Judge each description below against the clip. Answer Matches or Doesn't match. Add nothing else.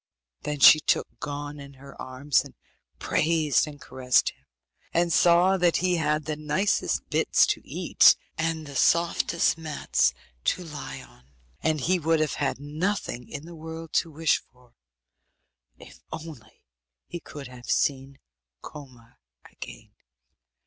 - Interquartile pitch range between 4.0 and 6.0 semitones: Doesn't match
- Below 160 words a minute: Matches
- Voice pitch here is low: Doesn't match